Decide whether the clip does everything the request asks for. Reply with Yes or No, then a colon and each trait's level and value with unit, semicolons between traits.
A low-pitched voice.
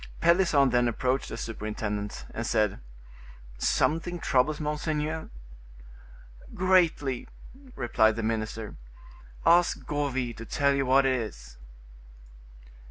Yes: low, 130 Hz